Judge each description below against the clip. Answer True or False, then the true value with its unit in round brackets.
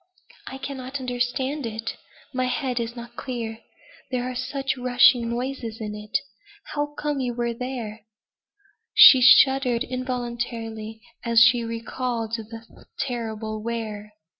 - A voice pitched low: False (240 Hz)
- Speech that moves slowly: True (120 wpm)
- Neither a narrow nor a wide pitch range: False (2.1 semitones)